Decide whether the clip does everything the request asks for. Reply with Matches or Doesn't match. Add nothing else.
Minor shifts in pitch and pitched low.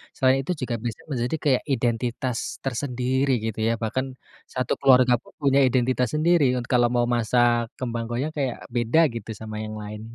Matches